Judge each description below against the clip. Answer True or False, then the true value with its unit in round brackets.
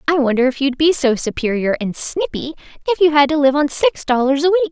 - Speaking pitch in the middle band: False (270 Hz)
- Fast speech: True (240 wpm)